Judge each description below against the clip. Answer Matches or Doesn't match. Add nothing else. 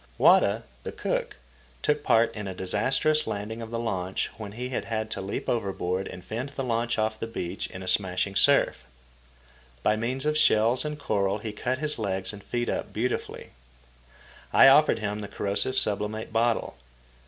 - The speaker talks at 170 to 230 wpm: Matches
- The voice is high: Doesn't match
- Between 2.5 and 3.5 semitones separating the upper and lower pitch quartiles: Matches